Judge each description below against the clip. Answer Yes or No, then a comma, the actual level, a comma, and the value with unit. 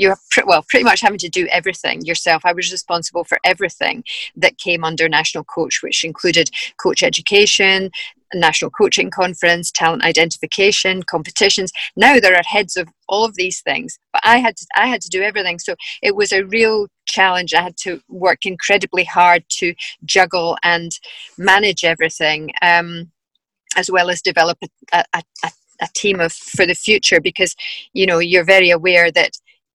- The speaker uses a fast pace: No, average, 175 wpm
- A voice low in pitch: No, medium, 180 Hz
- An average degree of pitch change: No, narrow, 2.1 semitones